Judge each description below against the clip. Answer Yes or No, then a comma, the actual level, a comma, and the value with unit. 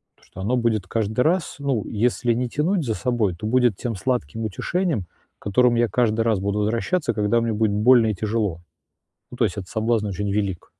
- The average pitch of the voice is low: Yes, low, 115 Hz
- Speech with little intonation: No, average, 3.0 semitones